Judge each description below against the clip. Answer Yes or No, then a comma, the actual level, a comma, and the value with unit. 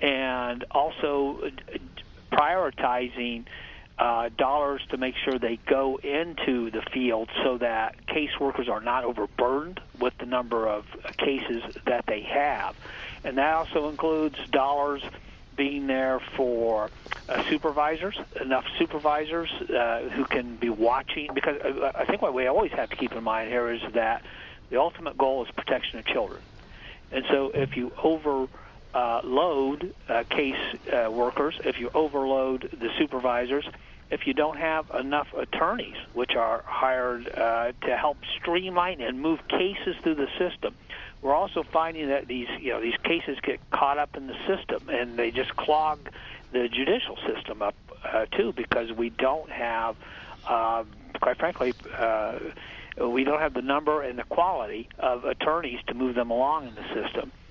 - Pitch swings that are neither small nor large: Yes, average, 3.8 semitones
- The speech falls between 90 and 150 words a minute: No, average, 160 wpm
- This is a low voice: Yes, low, 130 Hz